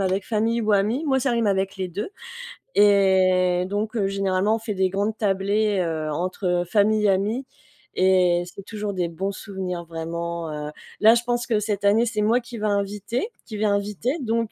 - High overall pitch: Yes, high, 200 Hz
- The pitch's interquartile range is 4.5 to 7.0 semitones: No, average, 2.7 semitones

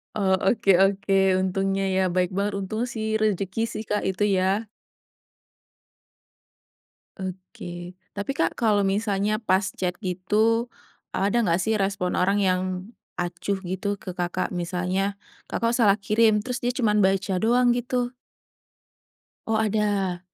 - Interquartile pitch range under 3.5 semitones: Yes, narrow, 2.5 semitones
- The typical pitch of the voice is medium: No, high, 195 Hz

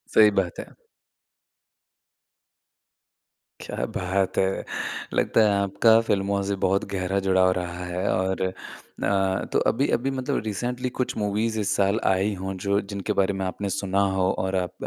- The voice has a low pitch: Yes, low, 100 Hz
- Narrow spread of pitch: Yes, narrow, 2.0 semitones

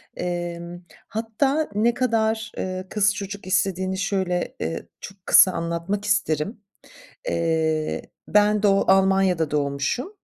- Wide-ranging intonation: No, average, 3.5 semitones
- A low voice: No, high, 190 Hz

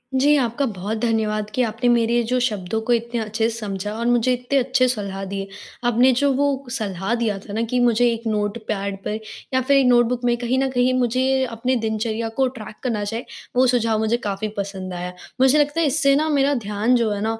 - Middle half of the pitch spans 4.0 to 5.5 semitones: No, average, 2.9 semitones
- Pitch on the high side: Yes, high, 230 Hz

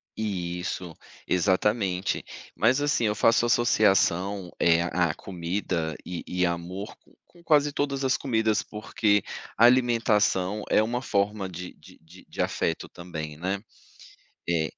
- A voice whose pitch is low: Yes, low, 100 Hz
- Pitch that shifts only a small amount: No, average, 4.2 semitones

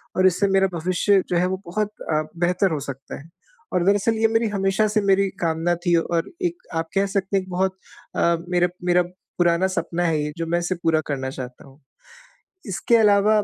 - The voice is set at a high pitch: No, medium, 180 Hz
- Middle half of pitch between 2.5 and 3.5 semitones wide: Yes, average, 2.9 semitones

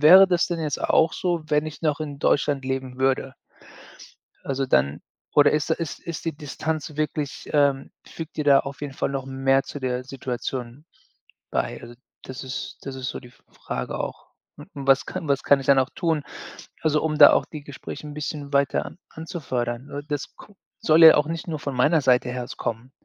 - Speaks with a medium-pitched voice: Yes, medium, 145 Hz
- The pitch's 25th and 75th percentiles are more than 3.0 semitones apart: No, average, 2.7 semitones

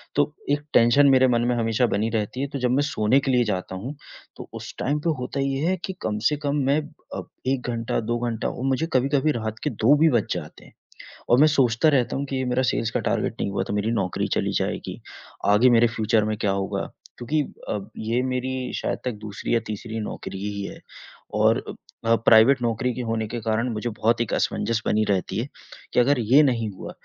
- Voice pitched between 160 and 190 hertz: No, low, 120 Hz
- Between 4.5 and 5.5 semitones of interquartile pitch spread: No, average, 3.6 semitones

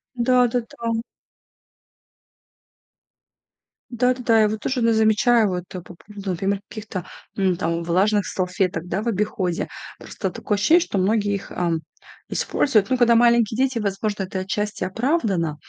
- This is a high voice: Yes, high, 210 Hz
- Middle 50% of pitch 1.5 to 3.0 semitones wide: No, average, 3.9 semitones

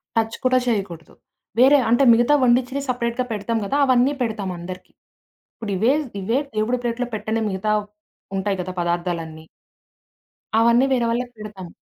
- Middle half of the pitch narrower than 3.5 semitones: No, average, 4.4 semitones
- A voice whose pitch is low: No, high, 225 Hz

